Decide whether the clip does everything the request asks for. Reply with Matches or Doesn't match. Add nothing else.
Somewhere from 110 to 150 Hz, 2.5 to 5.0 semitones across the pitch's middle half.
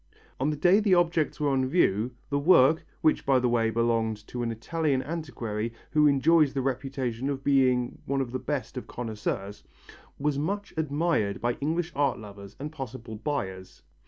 Matches